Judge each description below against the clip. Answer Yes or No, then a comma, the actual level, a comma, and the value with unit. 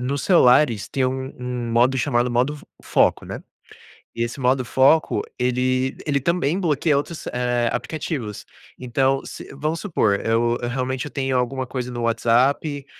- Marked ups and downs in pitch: No, narrow, 2.6 semitones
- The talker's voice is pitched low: Yes, low, 130 Hz